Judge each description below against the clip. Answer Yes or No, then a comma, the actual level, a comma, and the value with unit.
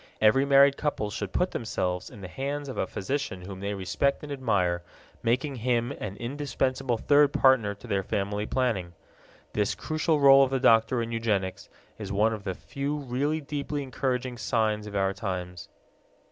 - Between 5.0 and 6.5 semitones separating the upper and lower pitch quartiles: Yes, wide, 5.5 semitones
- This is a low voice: Yes, low, 115 Hz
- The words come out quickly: No, average, 175 wpm